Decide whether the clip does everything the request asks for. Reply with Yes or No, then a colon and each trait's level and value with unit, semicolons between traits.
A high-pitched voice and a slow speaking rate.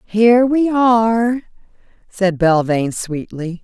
Yes: high, 205 Hz; slow, 100 wpm